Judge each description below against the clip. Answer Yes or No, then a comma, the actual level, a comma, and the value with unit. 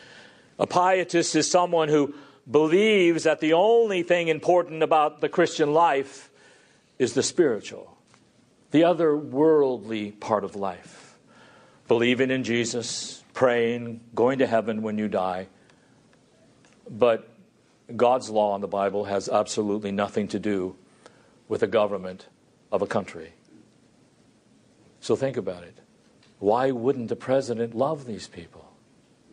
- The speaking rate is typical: No, slow, 125 wpm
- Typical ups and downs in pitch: No, wide, 6.7 semitones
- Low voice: Yes, low, 130 Hz